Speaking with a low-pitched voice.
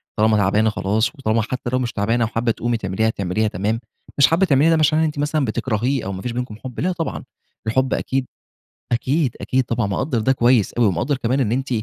Yes: low, 120 Hz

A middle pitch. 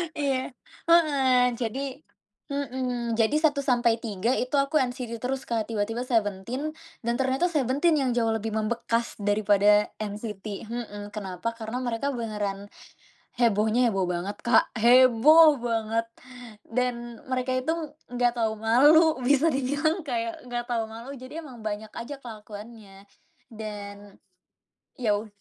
No: high, 235 Hz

